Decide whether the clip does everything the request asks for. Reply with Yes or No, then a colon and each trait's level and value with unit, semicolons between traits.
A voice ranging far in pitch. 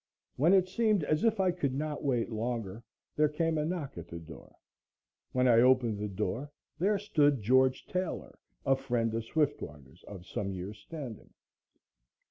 Yes: wide, 6.3 semitones